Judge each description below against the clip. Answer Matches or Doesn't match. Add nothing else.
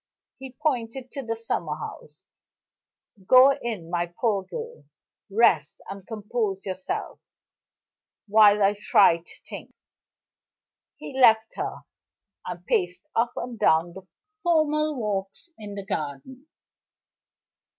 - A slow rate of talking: Matches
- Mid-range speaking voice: Doesn't match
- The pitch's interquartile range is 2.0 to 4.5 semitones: Doesn't match